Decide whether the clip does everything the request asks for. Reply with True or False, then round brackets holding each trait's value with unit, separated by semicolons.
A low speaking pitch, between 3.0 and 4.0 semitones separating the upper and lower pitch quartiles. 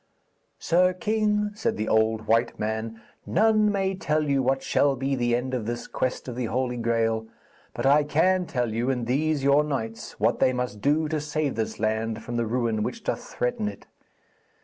False (125 Hz; 5.1 semitones)